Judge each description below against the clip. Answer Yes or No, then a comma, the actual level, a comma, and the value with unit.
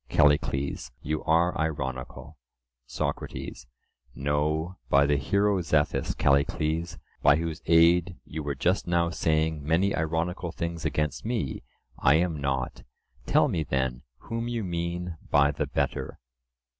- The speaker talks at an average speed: No, slow, 125 wpm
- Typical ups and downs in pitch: Yes, average, 3.1 semitones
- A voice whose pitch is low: Yes, very low, 80 Hz